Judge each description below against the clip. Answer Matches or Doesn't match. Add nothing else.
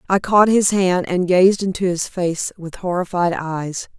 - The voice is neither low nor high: Matches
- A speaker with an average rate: Matches